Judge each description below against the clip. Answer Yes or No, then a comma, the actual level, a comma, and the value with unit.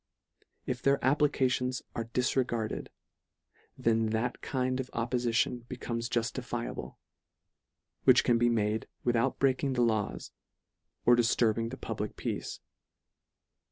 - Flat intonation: Yes, narrow, 1.8 semitones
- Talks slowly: Yes, slow, 125 wpm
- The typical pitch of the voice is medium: No, low, 120 Hz